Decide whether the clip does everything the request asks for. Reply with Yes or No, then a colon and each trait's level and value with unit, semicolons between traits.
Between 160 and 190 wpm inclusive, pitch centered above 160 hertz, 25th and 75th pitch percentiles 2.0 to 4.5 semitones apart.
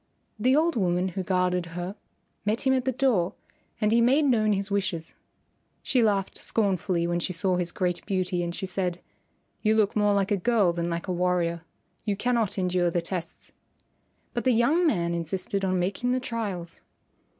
Yes: average, 185 wpm; high, 190 Hz; average, 4.0 semitones